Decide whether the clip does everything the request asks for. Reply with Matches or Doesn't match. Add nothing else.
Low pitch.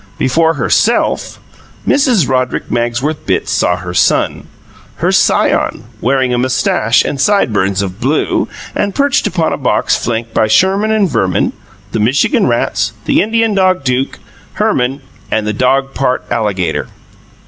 Matches